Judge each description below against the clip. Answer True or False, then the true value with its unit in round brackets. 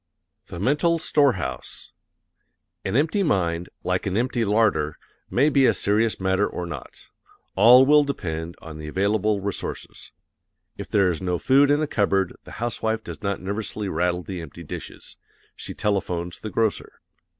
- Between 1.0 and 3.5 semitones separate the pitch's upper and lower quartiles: False (5.2 semitones)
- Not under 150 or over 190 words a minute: True (155 wpm)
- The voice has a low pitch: True (100 Hz)